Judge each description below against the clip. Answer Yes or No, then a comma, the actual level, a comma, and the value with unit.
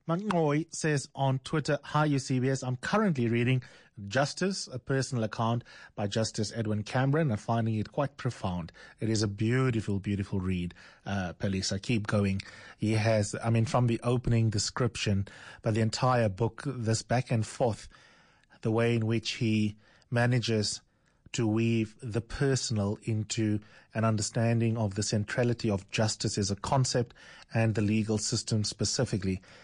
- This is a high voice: No, low, 115 Hz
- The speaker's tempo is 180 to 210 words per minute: No, average, 150 wpm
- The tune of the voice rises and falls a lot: No, average, 3.1 semitones